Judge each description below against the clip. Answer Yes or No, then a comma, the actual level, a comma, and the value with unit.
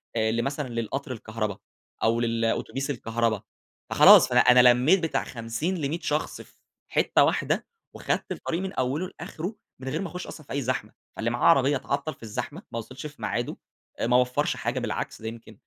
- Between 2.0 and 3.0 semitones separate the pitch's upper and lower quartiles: No, average, 4.2 semitones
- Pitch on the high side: No, low, 125 Hz